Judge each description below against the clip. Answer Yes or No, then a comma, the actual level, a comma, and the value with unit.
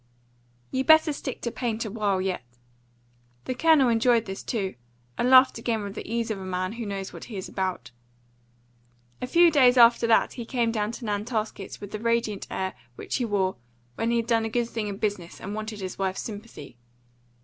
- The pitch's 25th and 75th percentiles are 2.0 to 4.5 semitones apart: Yes, average, 3.3 semitones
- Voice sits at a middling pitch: No, high, 225 Hz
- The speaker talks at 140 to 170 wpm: No, fast, 205 wpm